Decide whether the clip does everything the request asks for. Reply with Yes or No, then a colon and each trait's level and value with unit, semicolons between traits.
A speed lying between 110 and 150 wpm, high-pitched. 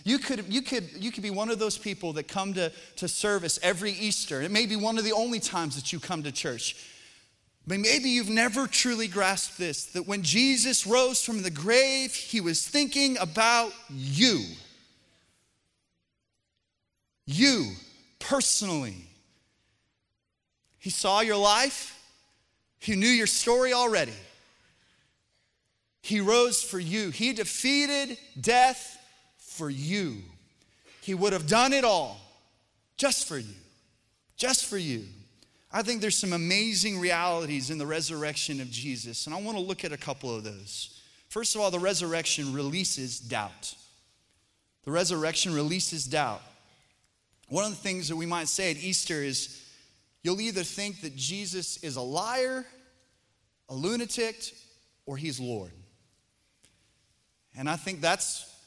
No: average, 145 wpm; medium, 175 Hz